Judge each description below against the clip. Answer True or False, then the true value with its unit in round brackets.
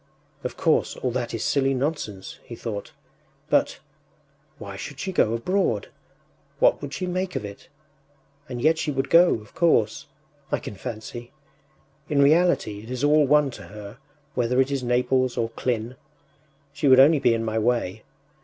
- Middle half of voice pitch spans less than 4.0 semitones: False (4.3 semitones)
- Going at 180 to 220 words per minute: False (170 wpm)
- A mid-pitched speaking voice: False (125 Hz)